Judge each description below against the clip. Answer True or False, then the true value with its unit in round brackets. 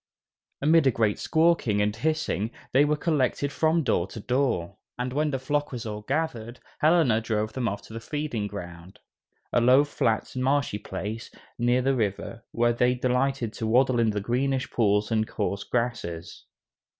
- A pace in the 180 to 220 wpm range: False (170 wpm)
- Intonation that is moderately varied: True (4.2 semitones)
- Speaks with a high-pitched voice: False (120 Hz)